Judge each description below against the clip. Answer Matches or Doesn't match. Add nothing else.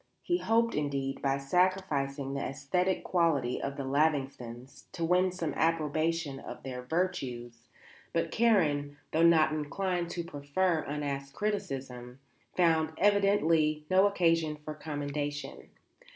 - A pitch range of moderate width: Matches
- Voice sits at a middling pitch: Matches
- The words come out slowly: Matches